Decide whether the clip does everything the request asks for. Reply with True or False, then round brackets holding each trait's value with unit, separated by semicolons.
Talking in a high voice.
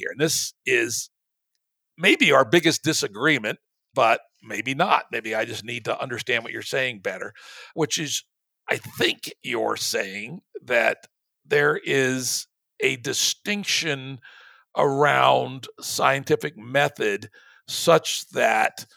False (140 Hz)